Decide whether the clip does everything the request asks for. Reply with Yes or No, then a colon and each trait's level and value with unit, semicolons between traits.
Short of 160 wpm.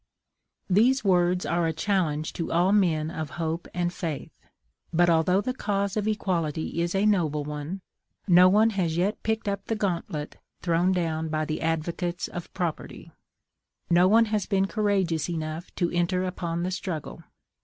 No: average, 165 wpm